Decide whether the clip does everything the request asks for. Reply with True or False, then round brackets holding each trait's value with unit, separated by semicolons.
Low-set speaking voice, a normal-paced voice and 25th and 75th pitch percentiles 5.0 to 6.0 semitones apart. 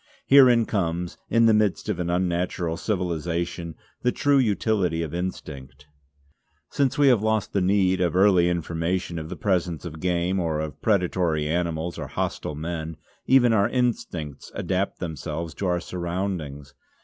False (90 Hz; 150 wpm; 3.4 semitones)